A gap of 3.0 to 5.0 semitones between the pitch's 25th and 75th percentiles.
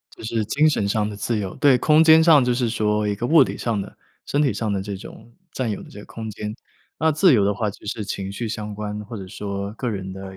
Yes: average, 3.5 semitones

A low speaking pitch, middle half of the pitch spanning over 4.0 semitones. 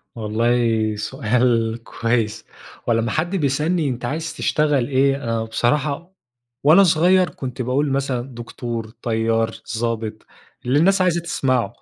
Yes: low, 125 Hz; average, 4.7 semitones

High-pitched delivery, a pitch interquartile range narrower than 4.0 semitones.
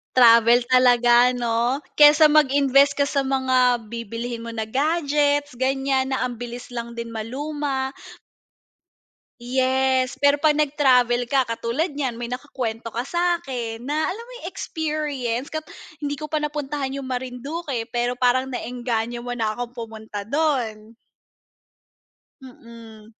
Yes: very high, 255 Hz; average, 3.3 semitones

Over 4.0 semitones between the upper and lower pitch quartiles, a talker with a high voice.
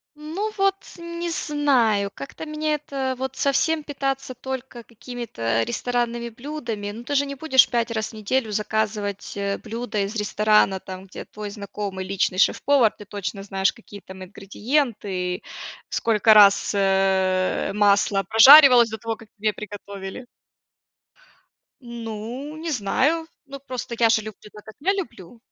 Yes: average, 4.8 semitones; high, 225 Hz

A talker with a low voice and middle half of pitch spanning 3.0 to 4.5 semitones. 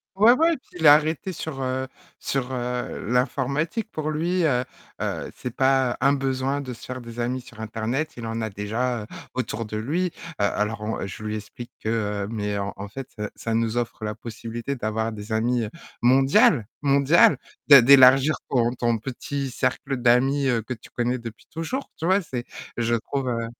Yes: low, 125 Hz; average, 3.5 semitones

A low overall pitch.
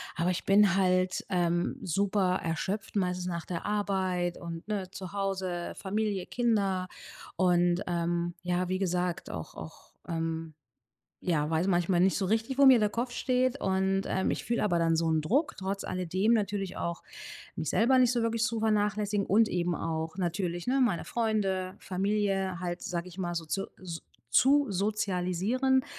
No: high, 190 Hz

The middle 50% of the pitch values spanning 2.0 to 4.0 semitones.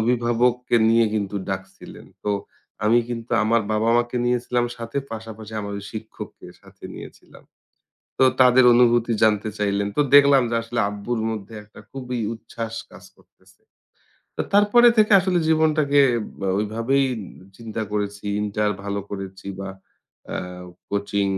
Yes: average, 3.0 semitones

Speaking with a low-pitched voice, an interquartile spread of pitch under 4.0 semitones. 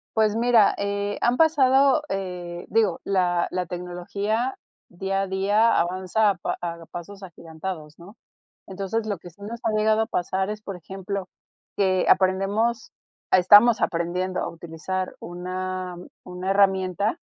No: high, 190 Hz; average, 2.9 semitones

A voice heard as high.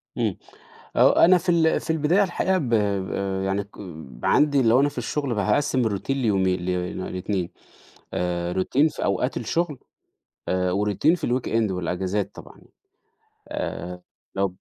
No: low, 105 Hz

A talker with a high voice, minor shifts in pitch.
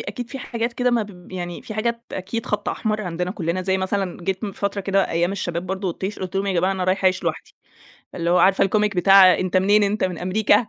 Yes: high, 195 Hz; narrow, 2.3 semitones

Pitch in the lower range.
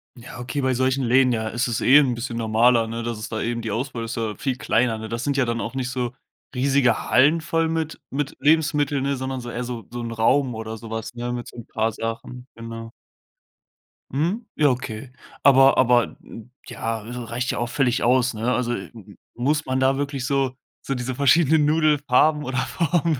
Yes: low, 125 Hz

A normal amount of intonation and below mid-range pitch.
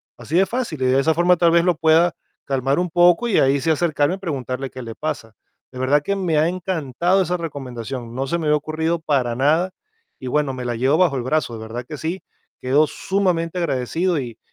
No: average, 4.8 semitones; medium, 155 Hz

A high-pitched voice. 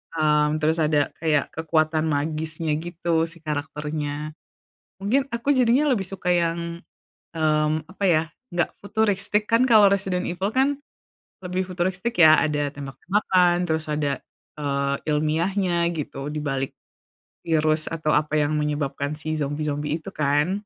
No: medium, 160 Hz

